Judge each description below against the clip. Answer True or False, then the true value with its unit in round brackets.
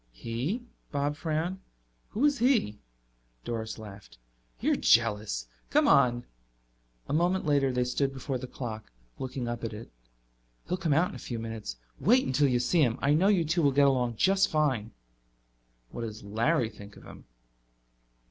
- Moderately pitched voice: False (130 Hz)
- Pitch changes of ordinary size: False (6.0 semitones)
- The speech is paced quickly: False (165 wpm)